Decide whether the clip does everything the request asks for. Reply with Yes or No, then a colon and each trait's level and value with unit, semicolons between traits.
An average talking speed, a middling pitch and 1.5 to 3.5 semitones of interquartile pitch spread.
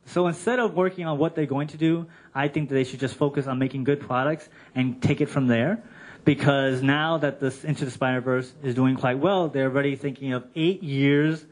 No: fast, 225 wpm; medium, 145 Hz; average, 2.9 semitones